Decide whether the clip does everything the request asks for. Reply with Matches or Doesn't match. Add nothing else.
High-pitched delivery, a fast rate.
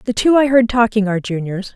Matches